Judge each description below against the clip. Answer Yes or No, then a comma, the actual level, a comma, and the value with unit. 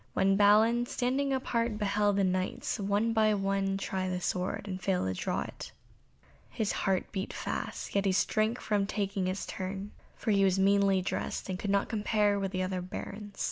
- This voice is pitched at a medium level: No, high, 200 Hz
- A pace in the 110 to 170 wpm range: No, average, 185 wpm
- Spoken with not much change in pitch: Yes, narrow, 1.8 semitones